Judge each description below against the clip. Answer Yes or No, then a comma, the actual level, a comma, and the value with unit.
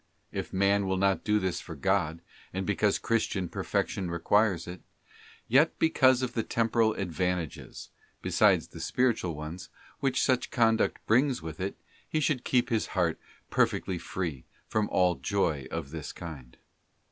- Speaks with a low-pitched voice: Yes, very low, 95 Hz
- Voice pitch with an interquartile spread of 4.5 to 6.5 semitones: Yes, average, 5.0 semitones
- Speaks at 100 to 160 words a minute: Yes, average, 155 wpm